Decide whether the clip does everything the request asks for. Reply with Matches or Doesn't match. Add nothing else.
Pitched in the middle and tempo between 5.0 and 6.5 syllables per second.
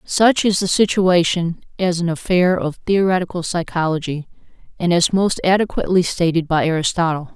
Matches